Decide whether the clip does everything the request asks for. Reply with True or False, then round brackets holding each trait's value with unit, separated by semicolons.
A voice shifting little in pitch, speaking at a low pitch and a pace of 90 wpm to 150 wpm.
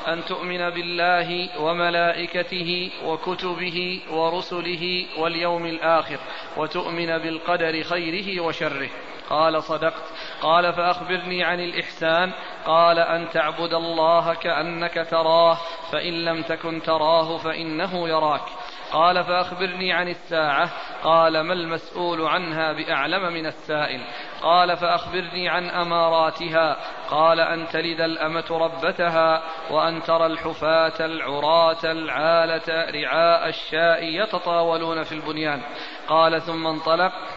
False (1.3 semitones; 165 Hz; 100 wpm)